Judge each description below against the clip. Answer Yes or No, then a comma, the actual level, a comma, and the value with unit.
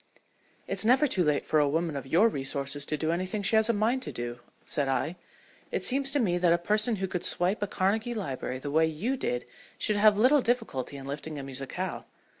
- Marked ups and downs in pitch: Yes, wide, 7.3 semitones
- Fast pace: Yes, fast, 225 wpm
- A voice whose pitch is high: No, medium, 175 Hz